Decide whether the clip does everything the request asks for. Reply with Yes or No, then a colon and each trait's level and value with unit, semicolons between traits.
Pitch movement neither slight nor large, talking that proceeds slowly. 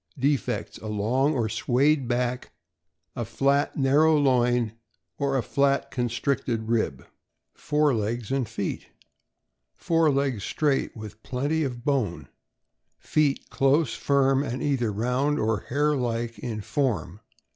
Yes: average, 3.4 semitones; slow, 130 wpm